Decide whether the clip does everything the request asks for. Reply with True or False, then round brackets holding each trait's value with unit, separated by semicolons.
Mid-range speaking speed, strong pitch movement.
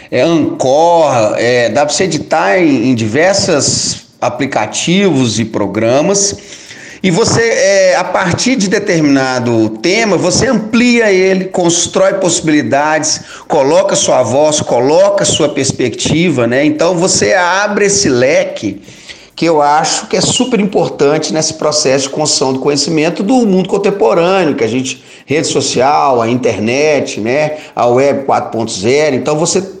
True (135 wpm; 6.1 semitones)